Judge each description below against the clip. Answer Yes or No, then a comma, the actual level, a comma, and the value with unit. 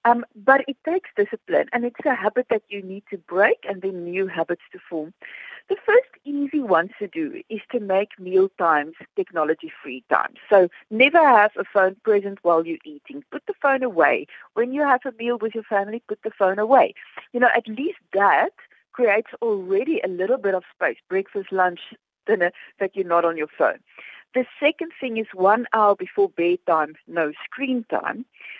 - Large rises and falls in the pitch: Yes, wide, 6.3 semitones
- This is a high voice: Yes, high, 215 Hz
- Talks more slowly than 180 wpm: No, average, 190 wpm